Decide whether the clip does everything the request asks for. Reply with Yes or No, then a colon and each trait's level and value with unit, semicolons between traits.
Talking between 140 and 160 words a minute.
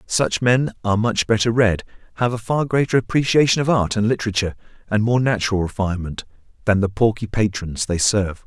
No: average, 175 wpm